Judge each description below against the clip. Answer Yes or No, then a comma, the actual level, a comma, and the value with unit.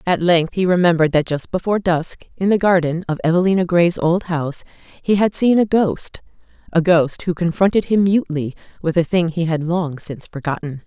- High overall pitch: No, medium, 170 Hz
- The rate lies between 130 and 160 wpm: No, average, 190 wpm